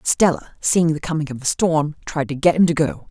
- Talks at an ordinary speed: No, fast, 250 wpm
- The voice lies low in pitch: No, medium, 155 Hz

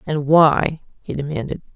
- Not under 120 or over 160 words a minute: Yes, slow, 135 wpm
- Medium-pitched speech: Yes, medium, 150 Hz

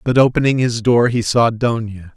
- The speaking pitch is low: Yes, low, 115 Hz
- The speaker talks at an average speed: Yes, average, 195 wpm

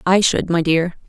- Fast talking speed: Yes, fast, 220 wpm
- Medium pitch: Yes, medium, 175 Hz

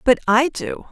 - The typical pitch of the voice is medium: No, high, 235 Hz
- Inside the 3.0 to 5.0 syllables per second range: Yes, 4.8 syllables/s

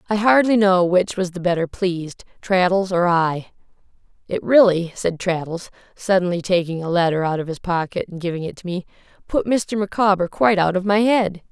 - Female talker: Yes, female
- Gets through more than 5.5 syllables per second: No, 5.3 syllables/s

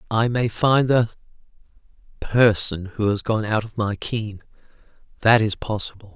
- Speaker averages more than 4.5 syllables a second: No, 4.4 syllables/s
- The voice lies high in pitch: No, low, 110 Hz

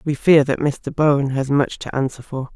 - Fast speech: Yes, fast, 235 wpm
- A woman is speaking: Yes, female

